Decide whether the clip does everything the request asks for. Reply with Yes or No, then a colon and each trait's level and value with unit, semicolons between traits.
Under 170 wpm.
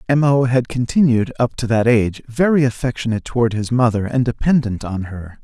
No: average, 190 wpm